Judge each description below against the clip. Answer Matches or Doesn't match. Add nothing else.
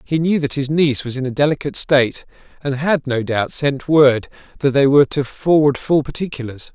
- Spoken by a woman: Doesn't match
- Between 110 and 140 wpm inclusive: Doesn't match